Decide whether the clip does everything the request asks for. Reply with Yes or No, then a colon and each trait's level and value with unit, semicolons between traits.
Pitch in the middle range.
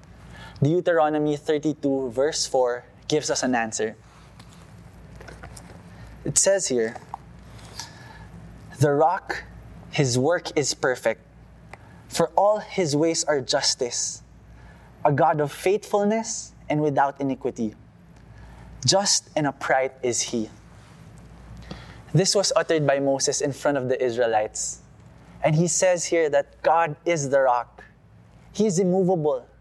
Yes: medium, 150 Hz